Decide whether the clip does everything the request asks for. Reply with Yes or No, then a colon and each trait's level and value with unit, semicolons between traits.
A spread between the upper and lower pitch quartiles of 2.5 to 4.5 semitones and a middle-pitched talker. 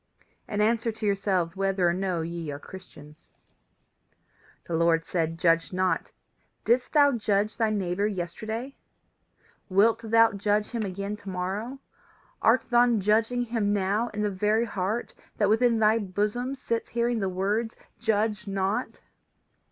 No: average, 3.3 semitones; high, 210 Hz